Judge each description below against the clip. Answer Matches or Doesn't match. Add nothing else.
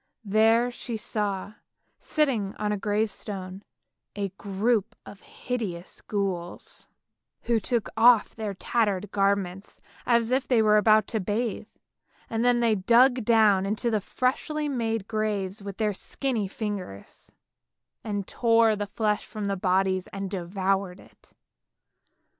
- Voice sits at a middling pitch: Doesn't match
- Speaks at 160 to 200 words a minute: Doesn't match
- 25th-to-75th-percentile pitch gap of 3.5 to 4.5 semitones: Doesn't match